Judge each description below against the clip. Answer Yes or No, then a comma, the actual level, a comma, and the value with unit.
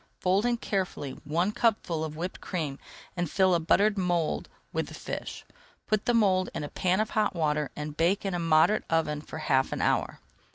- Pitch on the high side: No, medium, 175 Hz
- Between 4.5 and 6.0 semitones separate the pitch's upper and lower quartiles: No, average, 4.1 semitones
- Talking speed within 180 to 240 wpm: Yes, average, 200 wpm